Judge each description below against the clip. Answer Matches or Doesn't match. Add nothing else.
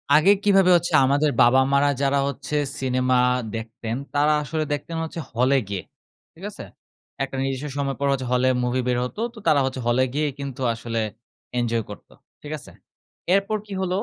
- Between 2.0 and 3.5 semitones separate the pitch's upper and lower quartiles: Matches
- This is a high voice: Doesn't match